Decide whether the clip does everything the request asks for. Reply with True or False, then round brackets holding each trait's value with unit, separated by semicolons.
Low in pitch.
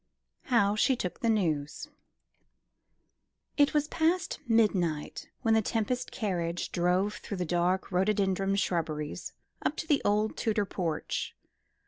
False (200 Hz)